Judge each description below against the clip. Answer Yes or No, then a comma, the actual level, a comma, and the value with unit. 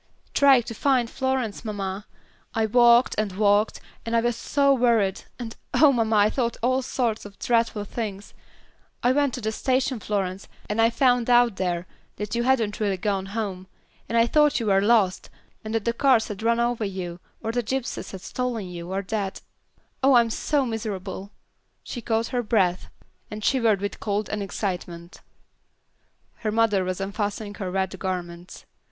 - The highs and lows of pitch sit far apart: No, average, 3.5 semitones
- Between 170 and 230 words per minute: Yes, average, 175 wpm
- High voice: Yes, high, 220 Hz